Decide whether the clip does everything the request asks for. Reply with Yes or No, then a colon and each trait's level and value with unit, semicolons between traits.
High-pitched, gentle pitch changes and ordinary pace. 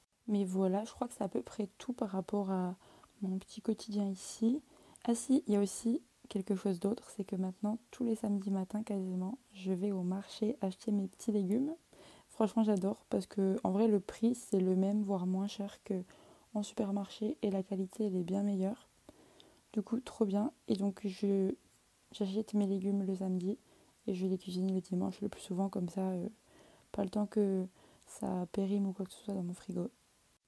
Yes: high, 200 Hz; narrow, 2.1 semitones; average, 205 wpm